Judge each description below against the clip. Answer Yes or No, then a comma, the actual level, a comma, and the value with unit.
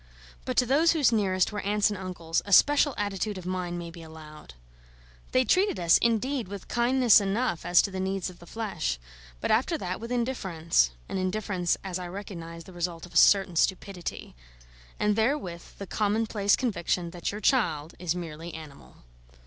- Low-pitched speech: No, high, 190 Hz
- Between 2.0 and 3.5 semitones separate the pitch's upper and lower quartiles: No, average, 4.2 semitones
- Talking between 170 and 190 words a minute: Yes, average, 180 wpm